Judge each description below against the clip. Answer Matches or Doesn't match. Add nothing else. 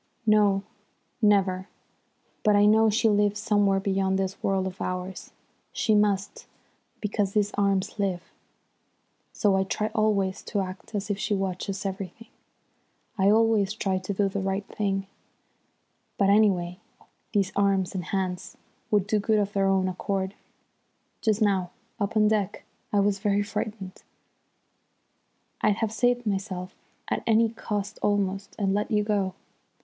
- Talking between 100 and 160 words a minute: Matches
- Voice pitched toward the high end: Matches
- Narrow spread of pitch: Matches